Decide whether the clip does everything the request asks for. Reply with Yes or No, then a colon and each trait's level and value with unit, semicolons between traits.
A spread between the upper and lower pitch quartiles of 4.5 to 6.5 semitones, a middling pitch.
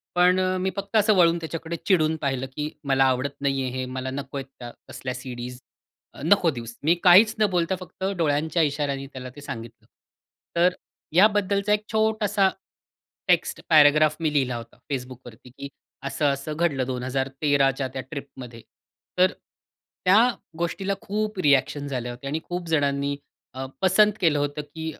Yes: average, 5.2 semitones; medium, 145 Hz